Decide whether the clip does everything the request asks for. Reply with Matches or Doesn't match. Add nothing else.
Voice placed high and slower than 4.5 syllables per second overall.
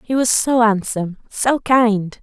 Matches